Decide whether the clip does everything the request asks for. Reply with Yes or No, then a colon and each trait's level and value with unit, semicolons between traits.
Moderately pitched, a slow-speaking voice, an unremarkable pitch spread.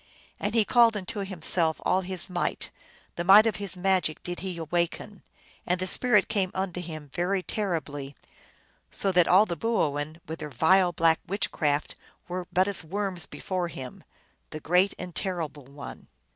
No: medium, 180 Hz; average, 170 wpm; average, 3.2 semitones